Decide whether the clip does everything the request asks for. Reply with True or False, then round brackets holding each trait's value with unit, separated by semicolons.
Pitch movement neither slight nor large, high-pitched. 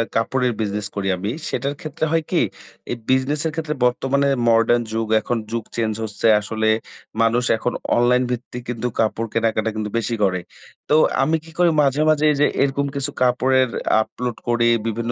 False (3.5 semitones; 120 Hz)